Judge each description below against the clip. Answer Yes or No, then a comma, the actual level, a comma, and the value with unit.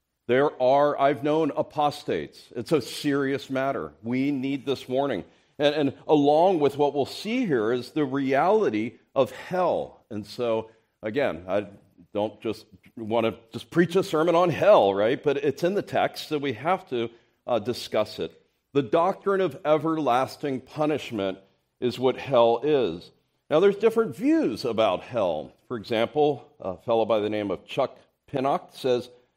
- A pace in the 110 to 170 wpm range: Yes, average, 160 wpm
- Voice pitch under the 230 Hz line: Yes, low, 135 Hz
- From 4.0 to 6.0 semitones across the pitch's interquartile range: Yes, average, 4.6 semitones